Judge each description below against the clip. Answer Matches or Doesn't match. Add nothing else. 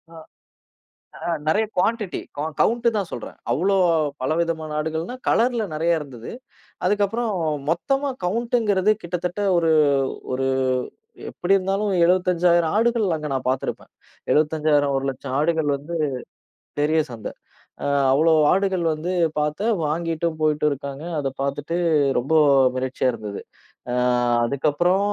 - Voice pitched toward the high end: Doesn't match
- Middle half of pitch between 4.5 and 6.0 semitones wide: Matches